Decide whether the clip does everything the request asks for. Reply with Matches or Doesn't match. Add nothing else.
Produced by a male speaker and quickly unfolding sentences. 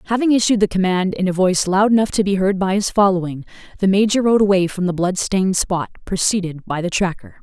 Doesn't match